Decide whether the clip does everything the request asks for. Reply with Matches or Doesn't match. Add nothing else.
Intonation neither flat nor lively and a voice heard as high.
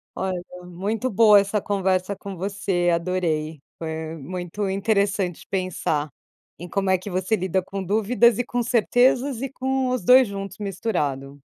Matches